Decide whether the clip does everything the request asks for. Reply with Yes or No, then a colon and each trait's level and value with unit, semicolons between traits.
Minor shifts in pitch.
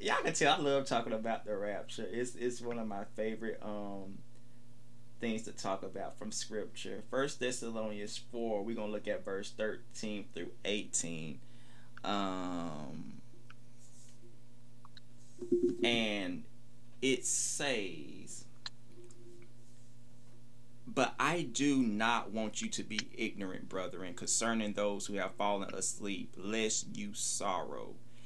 Yes: narrow, 2.3 semitones